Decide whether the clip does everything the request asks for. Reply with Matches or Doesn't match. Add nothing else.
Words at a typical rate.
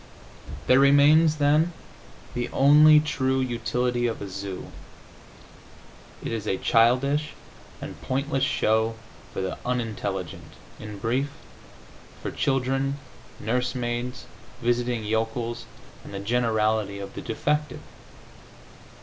Doesn't match